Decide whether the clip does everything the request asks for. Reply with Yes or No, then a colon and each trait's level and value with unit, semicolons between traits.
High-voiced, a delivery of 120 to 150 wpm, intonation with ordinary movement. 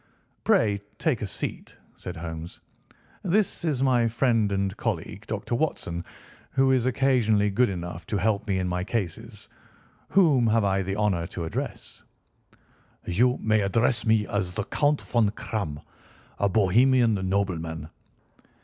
No: low, 105 Hz; average, 140 wpm; average, 4.4 semitones